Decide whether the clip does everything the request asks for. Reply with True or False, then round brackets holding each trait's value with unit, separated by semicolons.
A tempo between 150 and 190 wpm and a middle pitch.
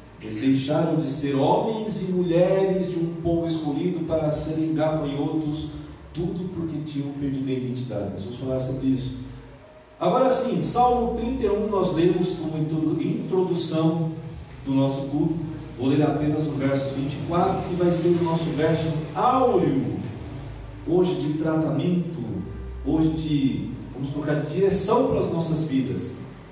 False (140 wpm; 155 Hz)